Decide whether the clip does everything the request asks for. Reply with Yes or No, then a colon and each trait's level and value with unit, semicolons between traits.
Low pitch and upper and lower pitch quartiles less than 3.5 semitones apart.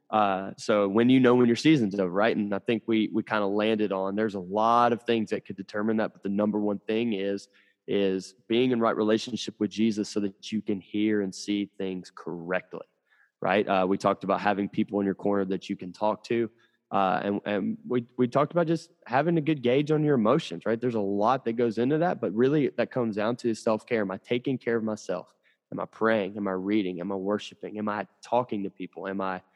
Yes: low, 105 Hz; average, 2.9 semitones